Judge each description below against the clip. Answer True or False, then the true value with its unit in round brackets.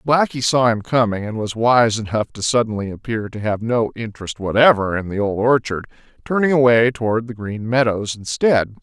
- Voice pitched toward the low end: True (115 Hz)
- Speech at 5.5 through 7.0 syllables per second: False (5.3 syllables/s)